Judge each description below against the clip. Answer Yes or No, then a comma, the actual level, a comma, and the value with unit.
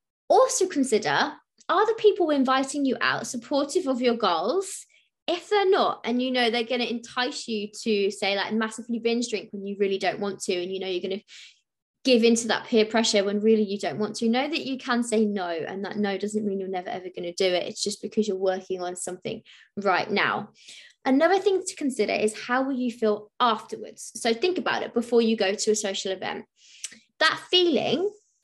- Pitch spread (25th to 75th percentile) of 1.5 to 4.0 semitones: No, average, 4.6 semitones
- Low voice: No, high, 225 Hz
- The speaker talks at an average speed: No, fast, 215 wpm